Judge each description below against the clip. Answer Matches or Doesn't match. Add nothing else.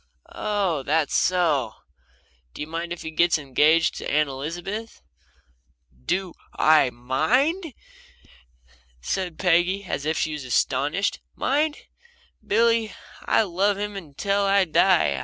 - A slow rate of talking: Matches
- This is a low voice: Doesn't match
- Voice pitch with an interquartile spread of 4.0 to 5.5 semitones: Matches